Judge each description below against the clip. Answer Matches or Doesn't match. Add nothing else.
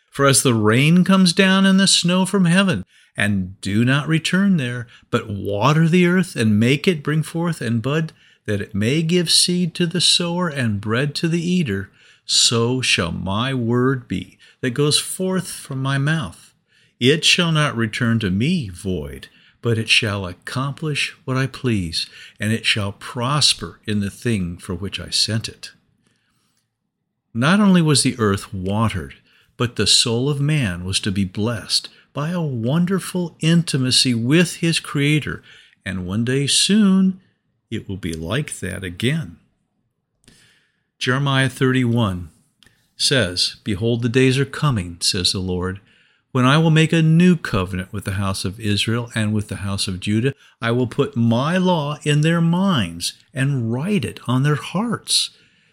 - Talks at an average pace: Matches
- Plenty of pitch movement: Matches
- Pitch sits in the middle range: Doesn't match